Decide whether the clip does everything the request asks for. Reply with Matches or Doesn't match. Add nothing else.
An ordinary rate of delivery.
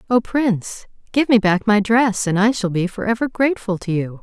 Doesn't match